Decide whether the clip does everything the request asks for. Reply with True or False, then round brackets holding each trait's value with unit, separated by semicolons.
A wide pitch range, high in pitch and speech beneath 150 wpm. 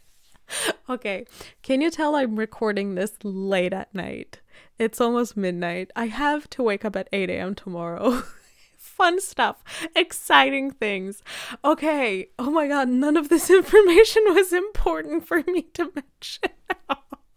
True (8.4 semitones; 265 Hz; 140 wpm)